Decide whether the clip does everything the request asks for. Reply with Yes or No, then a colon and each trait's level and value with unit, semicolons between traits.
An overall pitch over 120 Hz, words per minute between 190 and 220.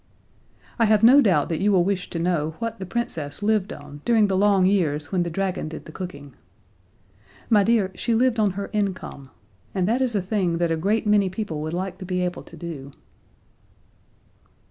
Yes: high, 190 Hz; average, 200 wpm